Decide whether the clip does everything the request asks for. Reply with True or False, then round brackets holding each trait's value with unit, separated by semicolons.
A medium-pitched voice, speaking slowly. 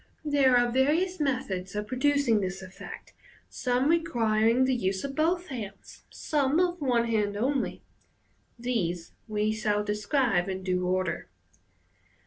False (235 Hz; 130 wpm)